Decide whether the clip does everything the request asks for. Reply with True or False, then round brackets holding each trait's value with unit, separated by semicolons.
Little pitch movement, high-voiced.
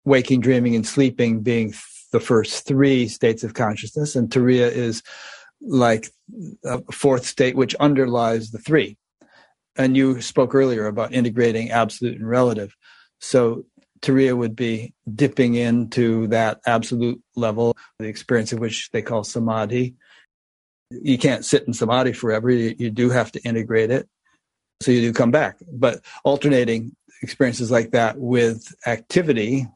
False (2.0 semitones; 120 Hz)